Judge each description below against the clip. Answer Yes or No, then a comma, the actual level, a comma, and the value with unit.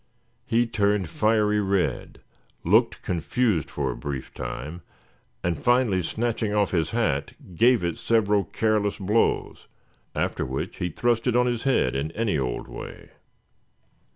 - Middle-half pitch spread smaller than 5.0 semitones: No, wide, 5.6 semitones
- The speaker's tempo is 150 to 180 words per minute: No, average, 140 wpm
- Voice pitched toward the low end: Yes, low, 105 Hz